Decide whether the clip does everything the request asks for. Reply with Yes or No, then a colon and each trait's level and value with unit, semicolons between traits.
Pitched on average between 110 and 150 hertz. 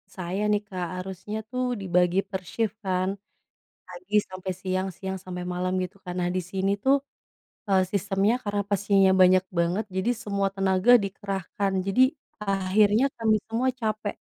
No: high, 195 Hz